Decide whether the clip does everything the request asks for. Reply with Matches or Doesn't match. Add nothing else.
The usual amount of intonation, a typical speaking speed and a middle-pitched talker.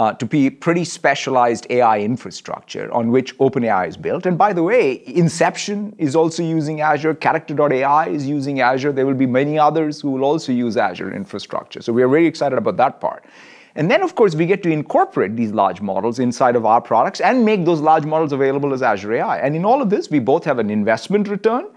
Doesn't match